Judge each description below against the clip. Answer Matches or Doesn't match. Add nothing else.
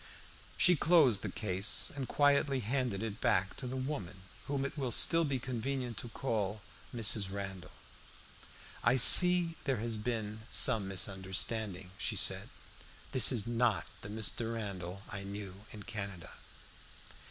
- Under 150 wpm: Matches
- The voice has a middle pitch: Doesn't match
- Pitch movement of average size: Matches